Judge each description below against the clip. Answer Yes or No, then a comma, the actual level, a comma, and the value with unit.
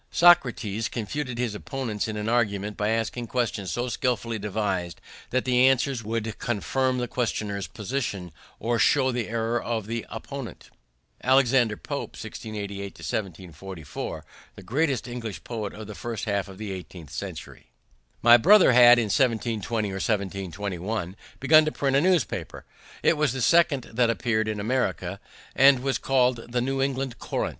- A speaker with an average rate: Yes, average, 150 wpm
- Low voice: Yes, low, 115 Hz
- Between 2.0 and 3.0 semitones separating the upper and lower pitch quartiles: No, average, 3.7 semitones